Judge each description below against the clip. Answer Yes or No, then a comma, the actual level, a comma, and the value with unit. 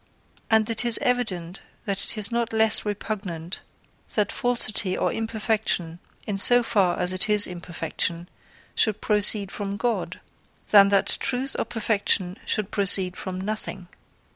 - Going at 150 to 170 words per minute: No, average, 140 wpm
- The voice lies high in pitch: Yes, high, 205 Hz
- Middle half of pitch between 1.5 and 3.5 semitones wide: Yes, average, 3.1 semitones